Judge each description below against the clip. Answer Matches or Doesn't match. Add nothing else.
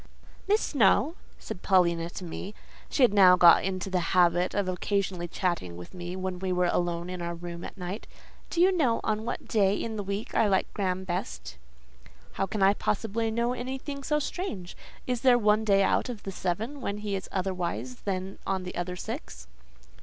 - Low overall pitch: Doesn't match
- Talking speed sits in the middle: Matches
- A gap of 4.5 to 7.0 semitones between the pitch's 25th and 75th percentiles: Doesn't match